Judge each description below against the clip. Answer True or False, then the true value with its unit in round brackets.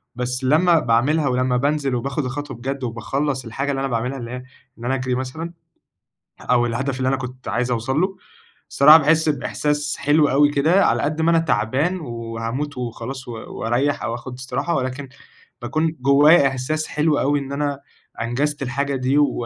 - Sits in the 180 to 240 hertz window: False (135 Hz)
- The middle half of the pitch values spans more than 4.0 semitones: False (2.9 semitones)